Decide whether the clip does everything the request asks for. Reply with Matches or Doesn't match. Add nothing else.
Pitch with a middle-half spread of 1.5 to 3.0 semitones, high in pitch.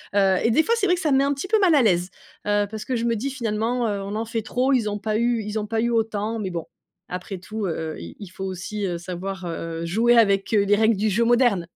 Doesn't match